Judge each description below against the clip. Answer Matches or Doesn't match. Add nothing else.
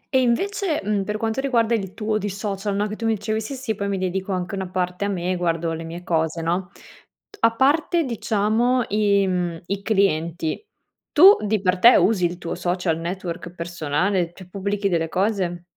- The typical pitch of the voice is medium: Doesn't match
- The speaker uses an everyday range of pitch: Matches